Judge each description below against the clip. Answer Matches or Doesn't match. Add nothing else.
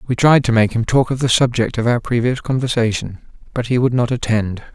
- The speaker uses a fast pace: Matches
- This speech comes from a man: Matches